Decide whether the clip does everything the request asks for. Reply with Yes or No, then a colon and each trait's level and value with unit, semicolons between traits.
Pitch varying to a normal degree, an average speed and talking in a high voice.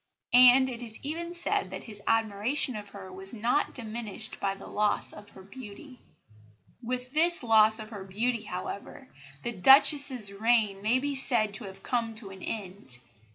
Yes: average, 4.0 semitones; average, 170 wpm; high, 225 Hz